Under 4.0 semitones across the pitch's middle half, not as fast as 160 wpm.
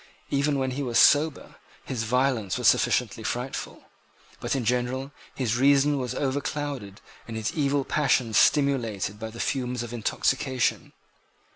Yes: average, 3.3 semitones; average, 140 wpm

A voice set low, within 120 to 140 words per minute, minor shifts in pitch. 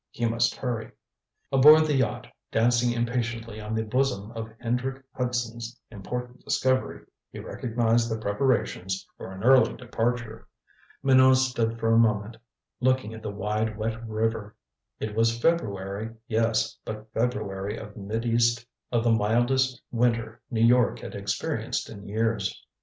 Yes: low, 115 Hz; slow, 135 wpm; narrow, 2.0 semitones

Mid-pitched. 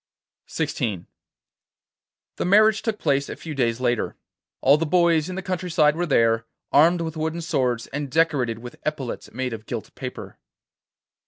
Yes: medium, 150 Hz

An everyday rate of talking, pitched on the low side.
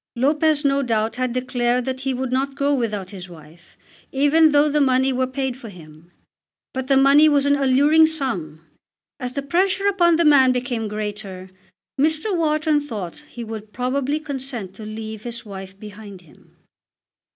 No: average, 170 wpm; very high, 255 Hz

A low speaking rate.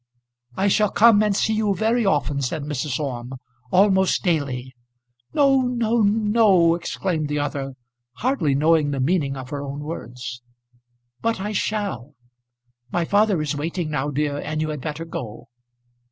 No: average, 155 wpm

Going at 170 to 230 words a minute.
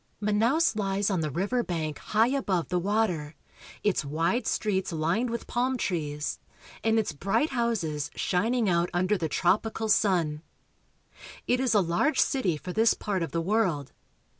No: average, 160 wpm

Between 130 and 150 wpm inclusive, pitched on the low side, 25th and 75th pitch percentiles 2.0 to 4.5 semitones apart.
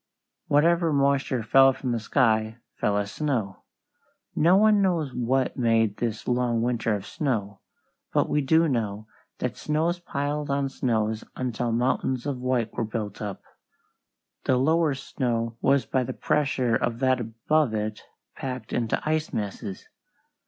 Yes: average, 145 wpm; low, 125 Hz; average, 4.1 semitones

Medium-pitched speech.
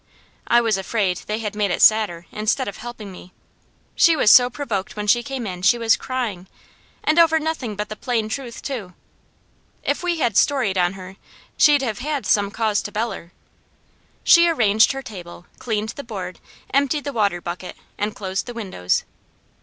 No: high, 220 Hz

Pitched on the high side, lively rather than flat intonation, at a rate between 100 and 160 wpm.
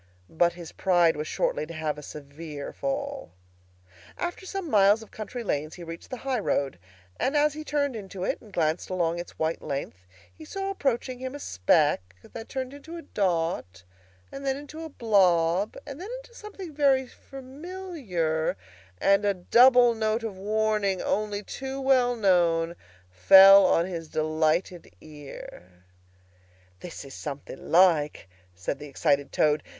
Yes: high, 195 Hz; wide, 8.8 semitones; average, 155 wpm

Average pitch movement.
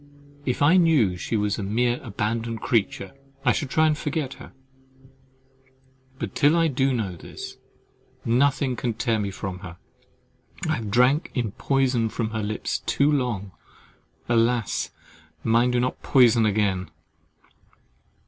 Yes: average, 3.9 semitones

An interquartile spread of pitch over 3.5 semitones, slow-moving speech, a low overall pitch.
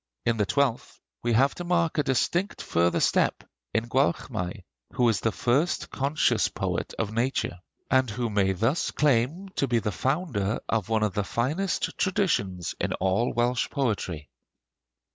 No: average, 5.0 semitones; average, 160 wpm; low, 120 Hz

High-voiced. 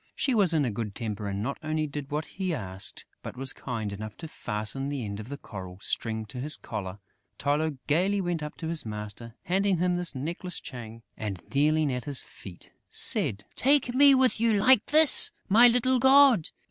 No: medium, 145 Hz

